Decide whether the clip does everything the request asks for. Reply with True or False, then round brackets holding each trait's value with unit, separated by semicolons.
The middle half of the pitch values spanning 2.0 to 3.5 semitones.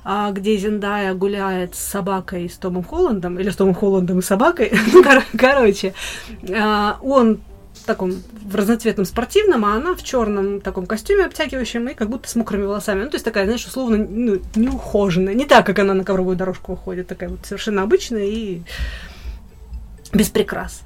True (2.8 semitones)